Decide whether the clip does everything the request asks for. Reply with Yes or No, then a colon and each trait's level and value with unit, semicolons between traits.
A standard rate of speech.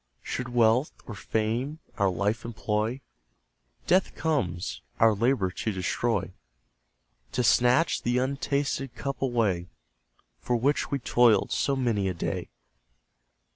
No: slow, 120 wpm